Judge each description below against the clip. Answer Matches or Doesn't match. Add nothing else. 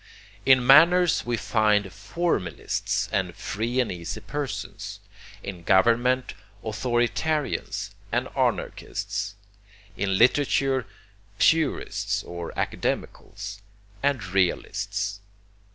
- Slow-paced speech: Matches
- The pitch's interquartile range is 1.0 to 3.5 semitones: Doesn't match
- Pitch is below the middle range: Matches